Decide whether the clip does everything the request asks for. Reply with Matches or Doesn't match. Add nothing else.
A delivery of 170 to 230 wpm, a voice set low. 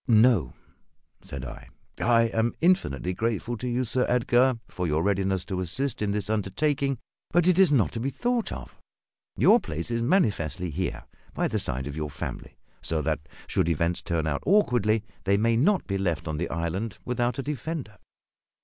Matches